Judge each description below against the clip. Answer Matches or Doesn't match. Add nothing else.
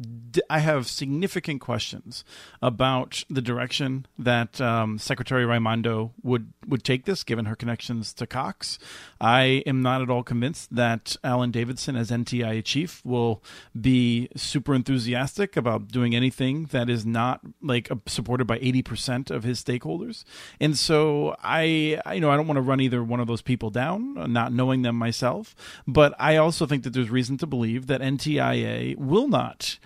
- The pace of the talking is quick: Doesn't match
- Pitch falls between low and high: Doesn't match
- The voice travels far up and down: Doesn't match